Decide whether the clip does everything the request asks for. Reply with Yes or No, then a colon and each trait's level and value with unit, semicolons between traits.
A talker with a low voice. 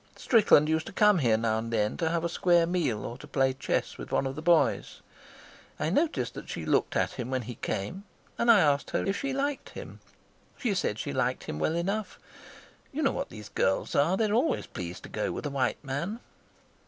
No: medium, 160 Hz